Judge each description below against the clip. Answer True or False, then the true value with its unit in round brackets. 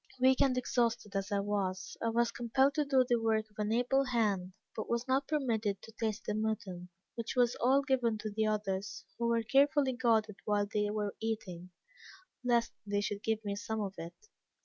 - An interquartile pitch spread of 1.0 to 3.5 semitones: True (2.9 semitones)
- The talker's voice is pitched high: True (220 Hz)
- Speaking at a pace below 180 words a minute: False (195 wpm)